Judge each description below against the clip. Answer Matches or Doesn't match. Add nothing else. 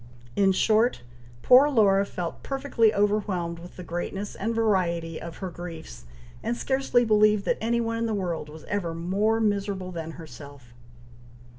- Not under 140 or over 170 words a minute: Matches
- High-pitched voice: Matches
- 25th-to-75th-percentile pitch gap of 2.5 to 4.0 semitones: Doesn't match